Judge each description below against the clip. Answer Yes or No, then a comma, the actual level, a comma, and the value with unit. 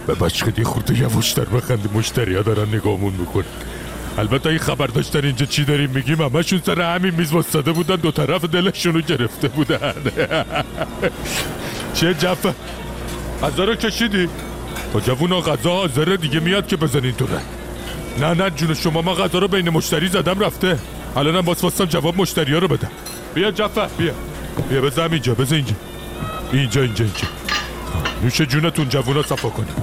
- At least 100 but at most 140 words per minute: No, fast, 155 wpm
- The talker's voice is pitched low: No, medium, 155 Hz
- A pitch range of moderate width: No, wide, 5.8 semitones